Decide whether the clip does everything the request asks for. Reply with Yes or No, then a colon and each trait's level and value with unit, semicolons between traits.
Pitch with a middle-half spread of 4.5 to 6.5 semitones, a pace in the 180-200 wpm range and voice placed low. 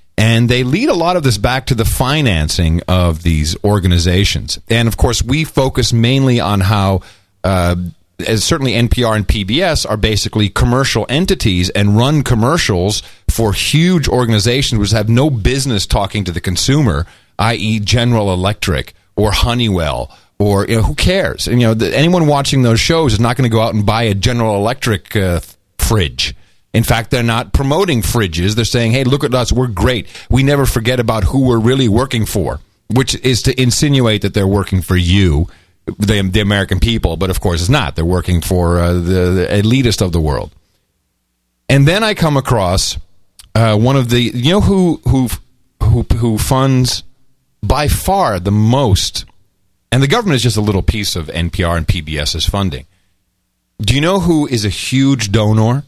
Yes: average, 5.2 semitones; average, 185 wpm; low, 110 Hz